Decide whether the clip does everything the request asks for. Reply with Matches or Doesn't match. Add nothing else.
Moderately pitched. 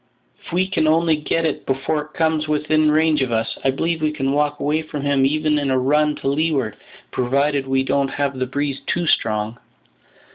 Matches